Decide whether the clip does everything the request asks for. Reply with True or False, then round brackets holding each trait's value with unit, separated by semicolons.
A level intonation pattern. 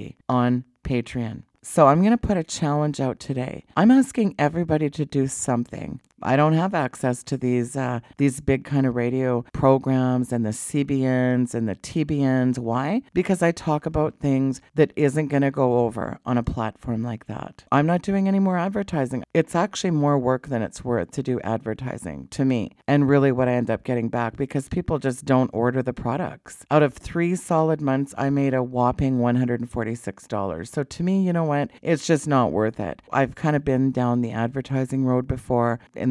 False (3.5 semitones)